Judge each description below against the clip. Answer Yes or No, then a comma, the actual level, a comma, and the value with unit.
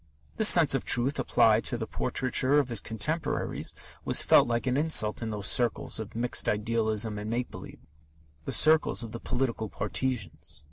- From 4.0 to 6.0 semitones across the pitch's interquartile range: No, average, 3.2 semitones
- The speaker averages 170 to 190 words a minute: Yes, average, 175 wpm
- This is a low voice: Yes, low, 120 Hz